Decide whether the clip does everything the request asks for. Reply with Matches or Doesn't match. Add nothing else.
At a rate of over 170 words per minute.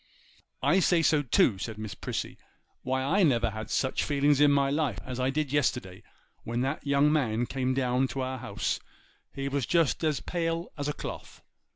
Matches